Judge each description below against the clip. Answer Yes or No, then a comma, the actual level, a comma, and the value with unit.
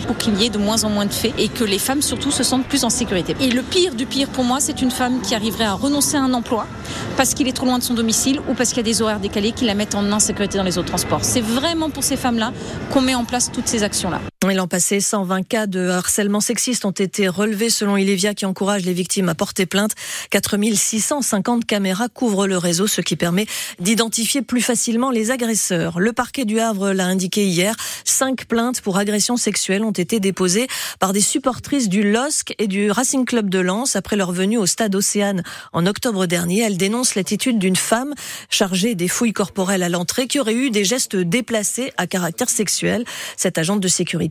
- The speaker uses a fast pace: Yes, fast, 225 wpm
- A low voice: No, high, 215 Hz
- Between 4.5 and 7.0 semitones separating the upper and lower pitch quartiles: No, average, 4.0 semitones